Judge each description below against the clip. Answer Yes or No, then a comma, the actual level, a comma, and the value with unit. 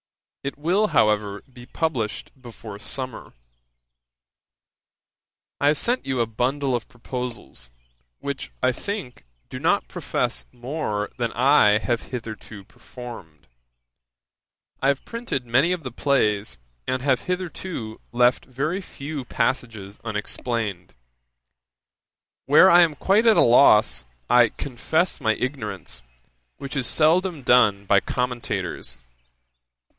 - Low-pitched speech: Yes, low, 125 Hz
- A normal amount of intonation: Yes, average, 4.8 semitones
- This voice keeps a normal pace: No, slow, 120 wpm